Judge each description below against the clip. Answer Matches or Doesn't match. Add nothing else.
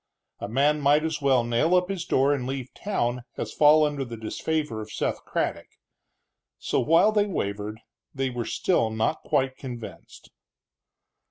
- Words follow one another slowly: Doesn't match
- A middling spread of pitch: Matches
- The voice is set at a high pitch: Doesn't match